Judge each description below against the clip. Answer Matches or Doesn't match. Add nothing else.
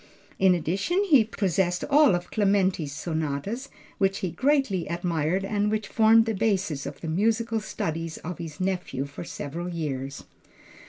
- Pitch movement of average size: Matches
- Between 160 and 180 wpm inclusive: Doesn't match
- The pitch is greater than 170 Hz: Matches